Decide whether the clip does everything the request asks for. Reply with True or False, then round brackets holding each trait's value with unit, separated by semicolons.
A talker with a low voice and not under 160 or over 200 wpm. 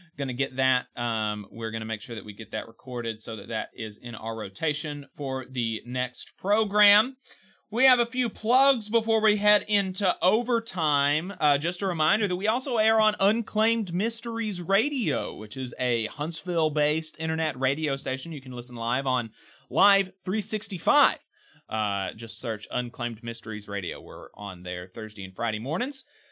False (150 Hz; 175 wpm)